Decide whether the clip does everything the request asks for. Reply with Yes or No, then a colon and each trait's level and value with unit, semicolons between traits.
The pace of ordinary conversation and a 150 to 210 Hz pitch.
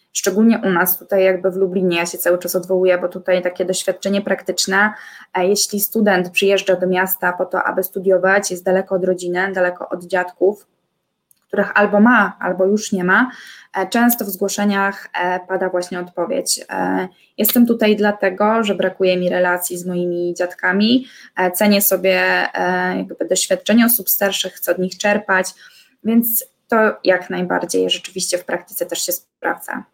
Yes: average, 150 wpm; high, 190 Hz